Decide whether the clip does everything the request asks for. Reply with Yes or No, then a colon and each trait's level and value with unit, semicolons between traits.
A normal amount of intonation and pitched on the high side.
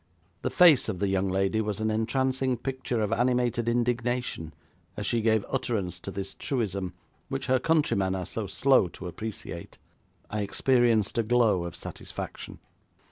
No: average, 4.2 semitones; low, 110 Hz